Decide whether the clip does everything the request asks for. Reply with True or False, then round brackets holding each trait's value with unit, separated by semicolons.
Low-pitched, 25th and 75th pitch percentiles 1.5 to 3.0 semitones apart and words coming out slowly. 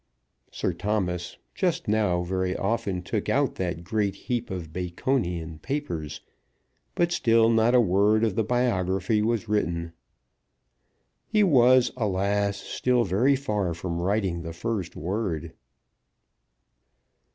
False (100 Hz; 4.7 semitones; 120 wpm)